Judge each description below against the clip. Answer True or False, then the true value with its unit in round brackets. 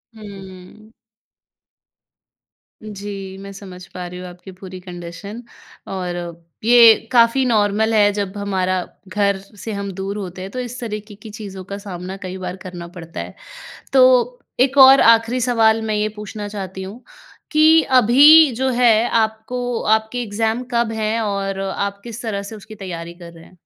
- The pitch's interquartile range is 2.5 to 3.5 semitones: True (3.2 semitones)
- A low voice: False (205 Hz)